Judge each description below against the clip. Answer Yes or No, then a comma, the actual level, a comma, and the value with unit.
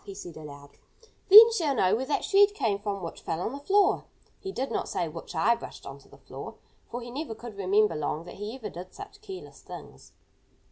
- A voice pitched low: No, high, 220 Hz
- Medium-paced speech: No, fast, 220 wpm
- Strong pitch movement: Yes, wide, 8.9 semitones